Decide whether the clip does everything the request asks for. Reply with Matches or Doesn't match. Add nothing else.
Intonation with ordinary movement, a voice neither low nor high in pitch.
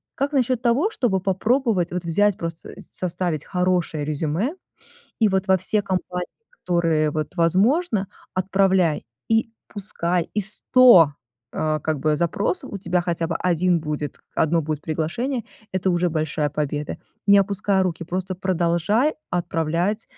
Matches